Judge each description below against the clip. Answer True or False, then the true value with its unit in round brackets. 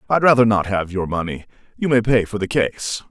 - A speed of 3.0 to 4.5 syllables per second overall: False (5.5 syllables/s)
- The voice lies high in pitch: False (105 Hz)